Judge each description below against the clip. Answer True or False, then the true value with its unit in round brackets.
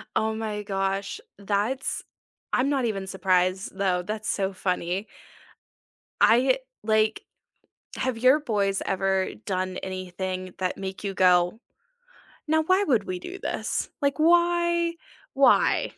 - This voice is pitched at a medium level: False (200 Hz)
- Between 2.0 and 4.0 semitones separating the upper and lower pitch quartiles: False (5.4 semitones)